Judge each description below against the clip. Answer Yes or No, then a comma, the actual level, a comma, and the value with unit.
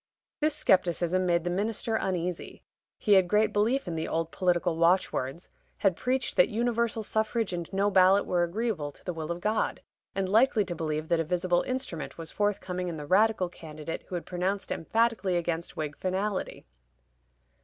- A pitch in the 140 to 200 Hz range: Yes, medium, 185 Hz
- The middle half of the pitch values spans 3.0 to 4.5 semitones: Yes, average, 3.7 semitones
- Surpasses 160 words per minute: Yes, average, 175 wpm